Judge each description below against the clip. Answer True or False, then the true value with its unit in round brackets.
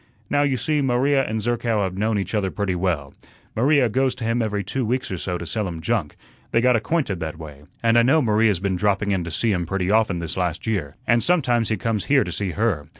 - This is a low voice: True (105 Hz)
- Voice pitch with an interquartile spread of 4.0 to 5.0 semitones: True (4.7 semitones)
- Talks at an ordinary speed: False (245 wpm)